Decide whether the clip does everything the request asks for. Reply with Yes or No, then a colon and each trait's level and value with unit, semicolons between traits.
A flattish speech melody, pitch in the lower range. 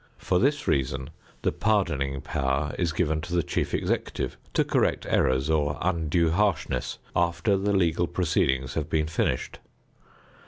No: average, 4.2 semitones; very low, 80 Hz